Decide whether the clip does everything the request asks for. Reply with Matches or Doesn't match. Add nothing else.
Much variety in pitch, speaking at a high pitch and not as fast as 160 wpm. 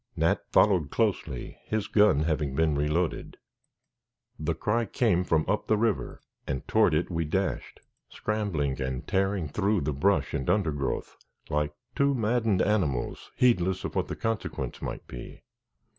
Doesn't match